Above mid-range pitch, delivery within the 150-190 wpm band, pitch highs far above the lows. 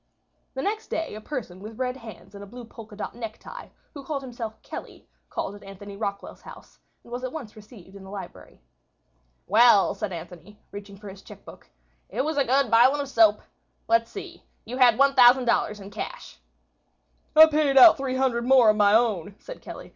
No: high, 230 Hz; average, 185 wpm; average, 4.5 semitones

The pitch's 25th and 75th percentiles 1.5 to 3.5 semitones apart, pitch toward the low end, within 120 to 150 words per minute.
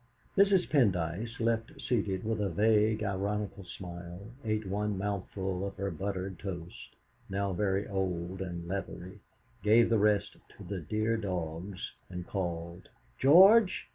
Yes: average, 2.9 semitones; low, 100 Hz; slow, 135 wpm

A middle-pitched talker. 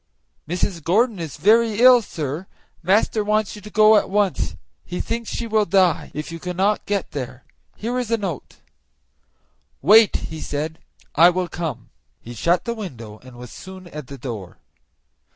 Yes: medium, 180 Hz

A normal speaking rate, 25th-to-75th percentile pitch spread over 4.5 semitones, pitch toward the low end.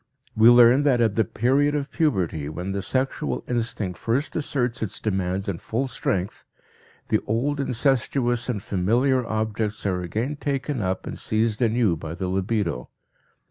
Yes: average, 155 wpm; average, 4.9 semitones; low, 115 Hz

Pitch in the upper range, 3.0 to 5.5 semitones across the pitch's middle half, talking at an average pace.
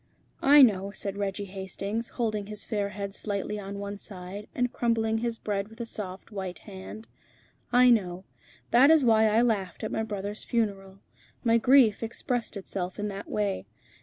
No: high, 210 Hz; narrow, 2.5 semitones; average, 170 wpm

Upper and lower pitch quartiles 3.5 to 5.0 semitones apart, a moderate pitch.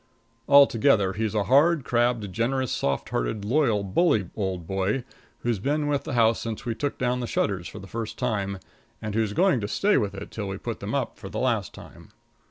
No: average, 4.6 semitones; low, 110 Hz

